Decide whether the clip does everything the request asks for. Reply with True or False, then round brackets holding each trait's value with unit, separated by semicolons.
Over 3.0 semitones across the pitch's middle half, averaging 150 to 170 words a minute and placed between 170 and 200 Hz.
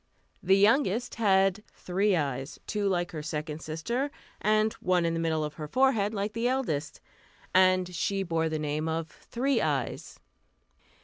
True (5.2 semitones; 160 wpm; 185 Hz)